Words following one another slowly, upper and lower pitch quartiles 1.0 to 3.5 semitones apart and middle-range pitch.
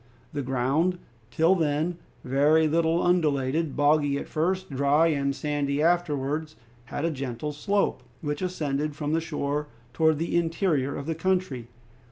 No: average, 145 wpm; average, 2.8 semitones; medium, 150 Hz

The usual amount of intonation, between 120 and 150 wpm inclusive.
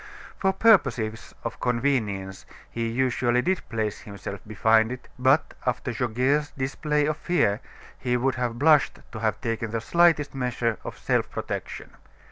Yes: average, 3.9 semitones; average, 145 wpm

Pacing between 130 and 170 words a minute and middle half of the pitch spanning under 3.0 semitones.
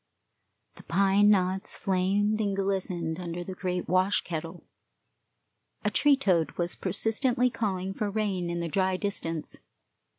Yes: slow, 135 wpm; narrow, 2.6 semitones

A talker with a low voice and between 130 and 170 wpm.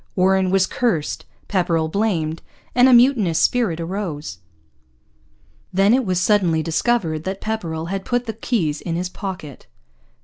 No: medium, 185 Hz; average, 140 wpm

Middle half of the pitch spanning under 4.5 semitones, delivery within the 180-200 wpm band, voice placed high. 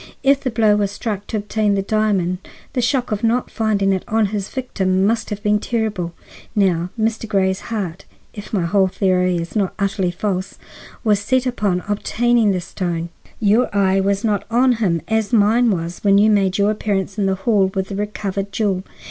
Yes: narrow, 2.4 semitones; average, 190 wpm; high, 205 Hz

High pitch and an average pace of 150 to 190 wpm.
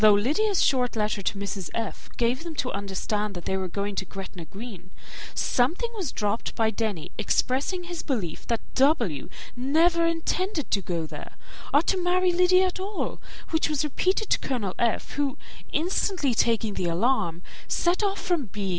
Yes: very high, 250 Hz; average, 170 wpm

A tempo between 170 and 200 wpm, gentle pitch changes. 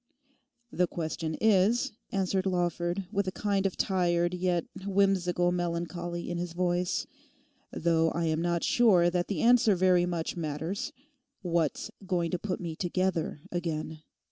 No: average, 140 wpm; narrow, 1.9 semitones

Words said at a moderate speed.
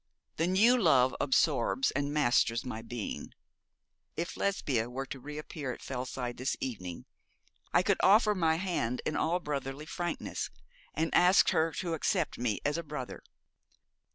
Yes: average, 155 wpm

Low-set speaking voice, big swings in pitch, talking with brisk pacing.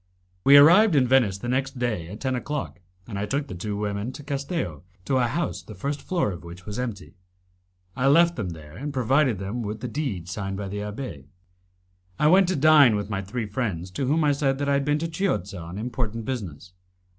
Yes: low, 120 Hz; wide, 6.0 semitones; fast, 215 wpm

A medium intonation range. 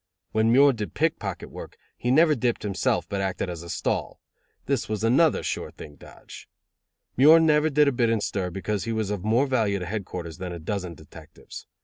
No: wide, 6.0 semitones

